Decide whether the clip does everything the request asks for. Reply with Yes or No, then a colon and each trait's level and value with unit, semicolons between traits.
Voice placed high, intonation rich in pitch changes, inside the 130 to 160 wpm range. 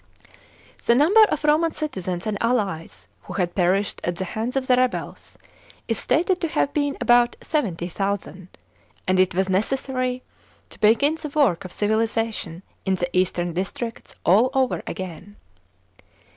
Yes: high, 220 Hz; wide, 6.0 semitones; average, 145 wpm